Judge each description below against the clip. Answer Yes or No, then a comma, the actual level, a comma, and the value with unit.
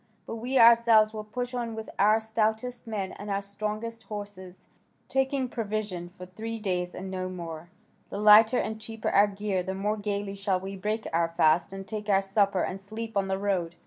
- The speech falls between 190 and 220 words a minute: Yes, average, 195 wpm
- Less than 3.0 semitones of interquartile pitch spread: Yes, narrow, 2.5 semitones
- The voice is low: No, high, 205 Hz